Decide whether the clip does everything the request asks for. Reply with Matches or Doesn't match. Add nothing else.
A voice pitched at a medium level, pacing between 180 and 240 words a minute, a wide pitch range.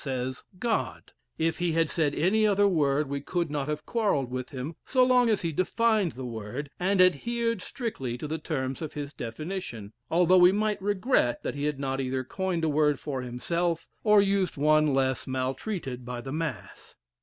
Matches